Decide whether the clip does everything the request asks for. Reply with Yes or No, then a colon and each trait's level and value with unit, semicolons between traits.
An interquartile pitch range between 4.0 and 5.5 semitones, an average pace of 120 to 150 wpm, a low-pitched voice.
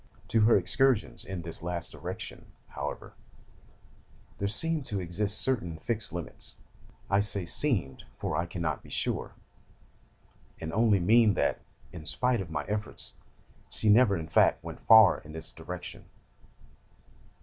Yes: average, 4.7 semitones; average, 140 wpm; low, 100 Hz